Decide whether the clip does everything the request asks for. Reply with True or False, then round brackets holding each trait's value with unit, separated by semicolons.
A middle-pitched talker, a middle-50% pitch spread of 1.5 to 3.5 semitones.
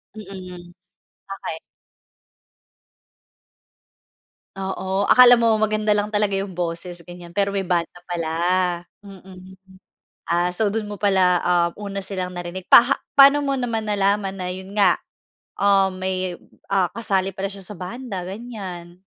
False (195 Hz; 2.4 semitones)